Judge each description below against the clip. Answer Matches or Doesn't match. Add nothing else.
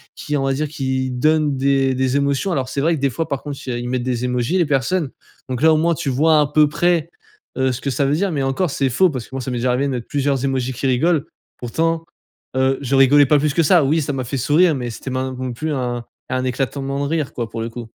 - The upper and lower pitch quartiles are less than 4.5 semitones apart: Matches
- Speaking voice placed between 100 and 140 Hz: Matches